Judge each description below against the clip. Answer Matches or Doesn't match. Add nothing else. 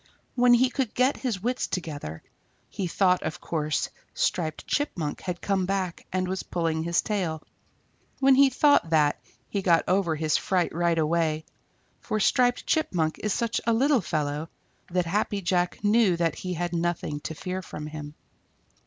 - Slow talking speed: Doesn't match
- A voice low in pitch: Doesn't match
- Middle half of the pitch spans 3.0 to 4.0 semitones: Doesn't match